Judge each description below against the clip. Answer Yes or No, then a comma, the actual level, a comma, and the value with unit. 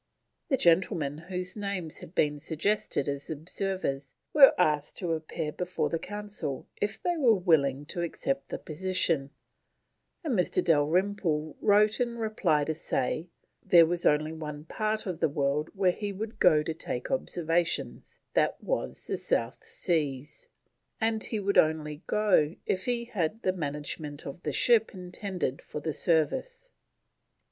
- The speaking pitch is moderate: Yes, medium, 175 Hz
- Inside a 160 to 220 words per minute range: No, average, 150 wpm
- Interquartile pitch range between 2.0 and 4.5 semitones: No, average, 5.3 semitones